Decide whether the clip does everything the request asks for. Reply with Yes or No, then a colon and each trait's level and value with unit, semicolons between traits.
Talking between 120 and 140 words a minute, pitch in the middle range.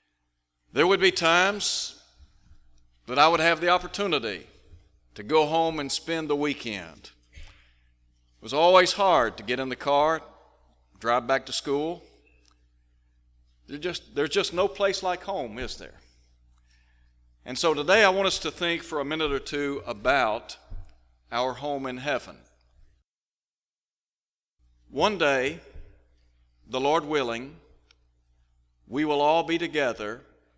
No: slow, 135 wpm; low, 115 Hz